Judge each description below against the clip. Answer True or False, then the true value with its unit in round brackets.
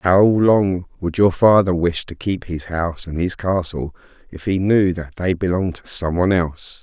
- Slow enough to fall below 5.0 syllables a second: True (4.8 syllables/s)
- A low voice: True (90 Hz)